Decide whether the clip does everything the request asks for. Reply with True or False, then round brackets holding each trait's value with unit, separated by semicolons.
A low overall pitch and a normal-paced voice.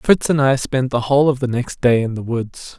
False (130 Hz; 280 wpm)